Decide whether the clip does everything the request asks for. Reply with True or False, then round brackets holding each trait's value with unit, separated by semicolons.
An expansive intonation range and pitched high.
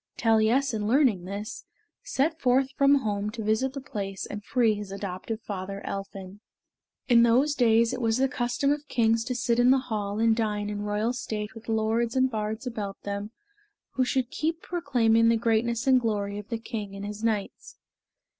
False (3.3 semitones; 225 Hz)